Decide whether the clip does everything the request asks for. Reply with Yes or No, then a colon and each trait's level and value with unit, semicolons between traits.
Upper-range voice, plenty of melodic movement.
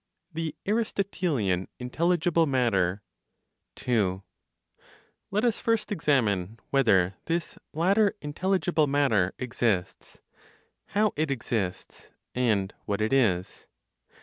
No: low, 135 Hz; wide, 9.0 semitones